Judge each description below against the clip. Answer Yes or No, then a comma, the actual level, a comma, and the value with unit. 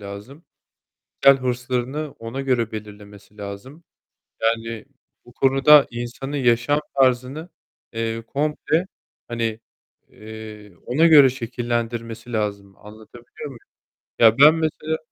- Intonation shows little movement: No, average, 3.7 semitones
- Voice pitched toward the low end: Yes, low, 120 Hz